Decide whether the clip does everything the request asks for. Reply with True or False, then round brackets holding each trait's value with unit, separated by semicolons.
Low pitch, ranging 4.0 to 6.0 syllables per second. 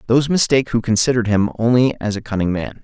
False (115 Hz; 7.4 syllables/s)